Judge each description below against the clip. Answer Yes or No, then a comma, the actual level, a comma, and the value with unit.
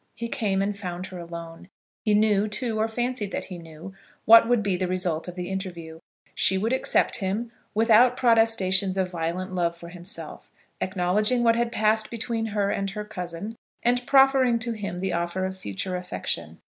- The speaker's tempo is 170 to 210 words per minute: Yes, average, 185 wpm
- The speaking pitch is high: Yes, high, 195 Hz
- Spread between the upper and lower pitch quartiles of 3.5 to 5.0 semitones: Yes, average, 3.9 semitones